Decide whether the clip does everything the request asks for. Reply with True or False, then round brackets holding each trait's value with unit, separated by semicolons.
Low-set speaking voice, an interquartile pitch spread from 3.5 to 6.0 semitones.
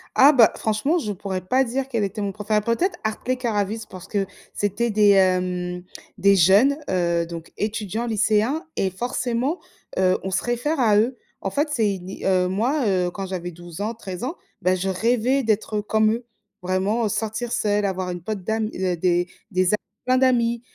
False (210 Hz; 4.1 semitones)